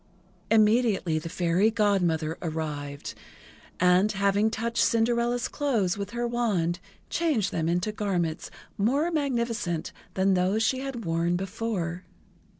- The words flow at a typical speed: No, slow, 120 wpm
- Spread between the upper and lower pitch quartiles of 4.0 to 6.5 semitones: Yes, average, 5.2 semitones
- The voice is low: No, high, 200 Hz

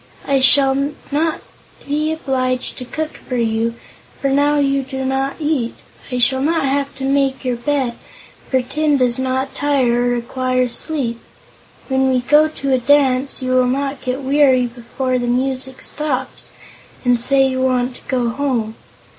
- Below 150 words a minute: No, average, 165 wpm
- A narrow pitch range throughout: Yes, narrow, 1.9 semitones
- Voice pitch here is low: No, very high, 265 Hz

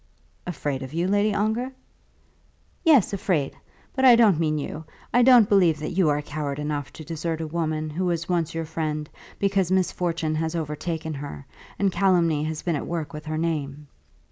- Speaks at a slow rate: No, average, 180 wpm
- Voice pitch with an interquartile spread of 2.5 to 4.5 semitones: Yes, average, 3.5 semitones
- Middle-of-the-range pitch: Yes, medium, 165 Hz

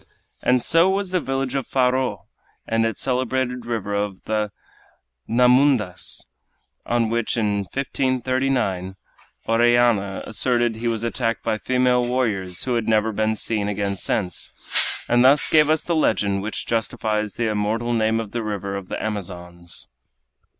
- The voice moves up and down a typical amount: Yes, average, 3.4 semitones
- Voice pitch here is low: Yes, low, 115 Hz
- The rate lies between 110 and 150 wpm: Yes, average, 145 wpm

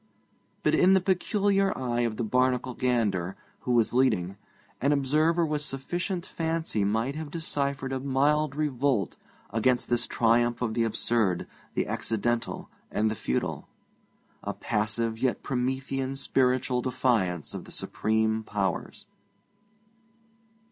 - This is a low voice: Yes, low, 125 Hz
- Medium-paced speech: No, slow, 125 wpm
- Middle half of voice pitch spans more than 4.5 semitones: No, average, 4.0 semitones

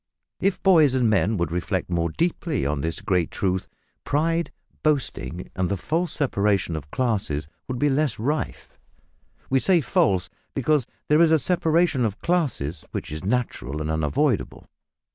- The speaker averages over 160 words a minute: No, average, 155 wpm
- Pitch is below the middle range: Yes, low, 115 Hz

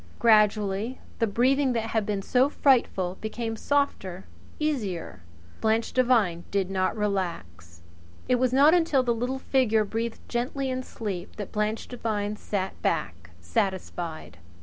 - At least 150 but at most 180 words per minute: No, slow, 135 wpm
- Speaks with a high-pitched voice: Yes, high, 220 Hz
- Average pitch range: Yes, average, 4.7 semitones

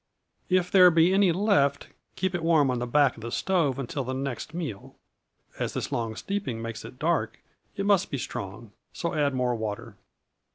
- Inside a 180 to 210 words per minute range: Yes, average, 190 wpm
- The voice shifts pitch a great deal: Yes, wide, 6.9 semitones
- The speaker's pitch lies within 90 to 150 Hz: Yes, medium, 140 Hz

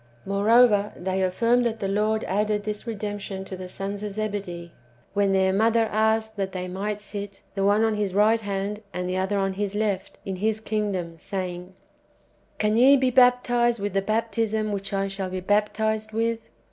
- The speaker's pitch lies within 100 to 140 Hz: No, high, 205 Hz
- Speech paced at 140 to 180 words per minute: No, average, 190 wpm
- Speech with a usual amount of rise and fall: No, narrow, 2.1 semitones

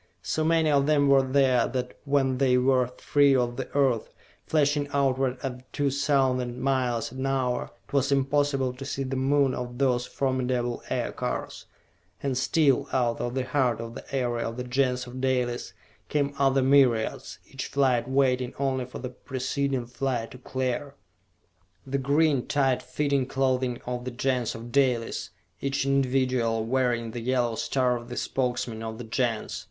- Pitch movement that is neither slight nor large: No, narrow, 1.8 semitones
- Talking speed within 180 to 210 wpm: No, average, 165 wpm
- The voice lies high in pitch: No, low, 130 Hz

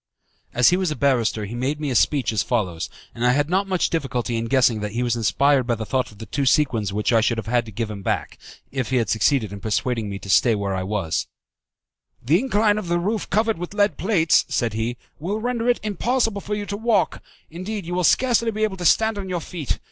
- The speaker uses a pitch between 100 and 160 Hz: Yes, low, 135 Hz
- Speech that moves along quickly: Yes, fast, 245 wpm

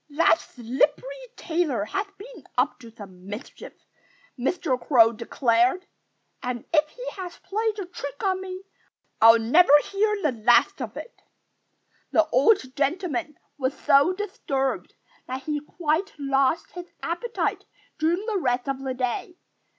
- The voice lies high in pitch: Yes, very high, 300 Hz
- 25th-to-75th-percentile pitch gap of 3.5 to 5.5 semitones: No, wide, 6.6 semitones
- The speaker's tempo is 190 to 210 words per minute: No, average, 140 wpm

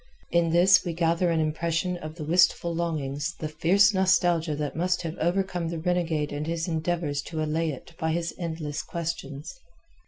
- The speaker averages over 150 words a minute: Yes, average, 175 wpm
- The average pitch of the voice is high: No, medium, 165 Hz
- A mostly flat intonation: Yes, narrow, 2.0 semitones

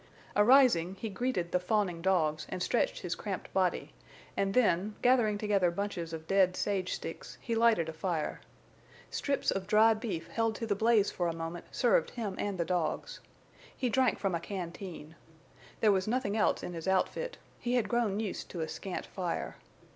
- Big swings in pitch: No, average, 4.4 semitones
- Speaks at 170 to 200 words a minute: Yes, average, 180 wpm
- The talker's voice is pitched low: No, high, 195 Hz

